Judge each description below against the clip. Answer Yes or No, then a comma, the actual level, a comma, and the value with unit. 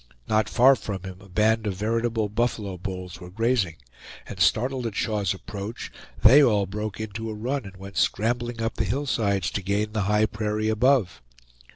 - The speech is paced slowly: No, average, 180 wpm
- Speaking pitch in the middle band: No, low, 105 Hz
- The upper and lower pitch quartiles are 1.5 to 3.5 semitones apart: Yes, average, 2.7 semitones